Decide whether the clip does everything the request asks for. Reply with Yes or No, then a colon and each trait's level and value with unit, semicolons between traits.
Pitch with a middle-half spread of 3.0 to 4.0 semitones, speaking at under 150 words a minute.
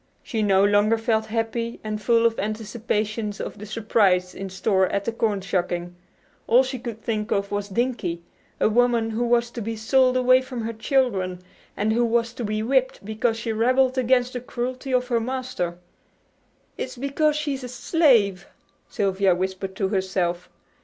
No: average, 3.7 semitones; average, 175 wpm